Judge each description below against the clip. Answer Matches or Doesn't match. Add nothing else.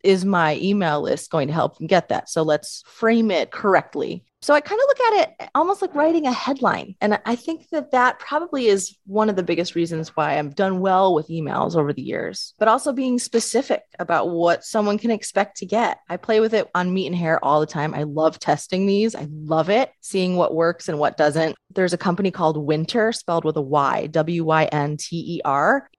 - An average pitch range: Doesn't match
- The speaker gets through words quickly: Matches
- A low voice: Doesn't match